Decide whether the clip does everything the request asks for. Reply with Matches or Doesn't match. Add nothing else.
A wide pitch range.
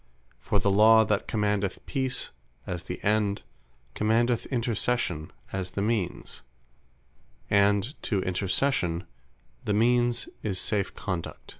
Doesn't match